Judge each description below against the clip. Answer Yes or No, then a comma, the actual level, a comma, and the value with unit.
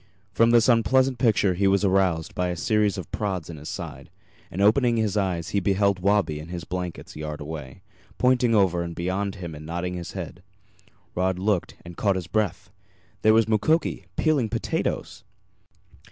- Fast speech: No, average, 180 wpm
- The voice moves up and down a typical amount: Yes, average, 3.7 semitones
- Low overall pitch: Yes, very low, 95 Hz